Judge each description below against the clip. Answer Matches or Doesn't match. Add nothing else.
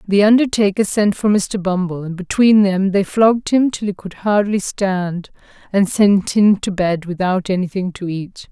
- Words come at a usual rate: Matches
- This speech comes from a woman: Matches